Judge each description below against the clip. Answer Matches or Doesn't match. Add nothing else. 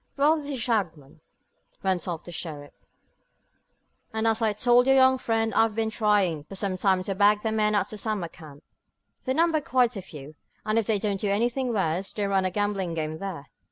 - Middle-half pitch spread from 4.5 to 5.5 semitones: Doesn't match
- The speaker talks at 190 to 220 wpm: Matches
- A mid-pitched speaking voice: Doesn't match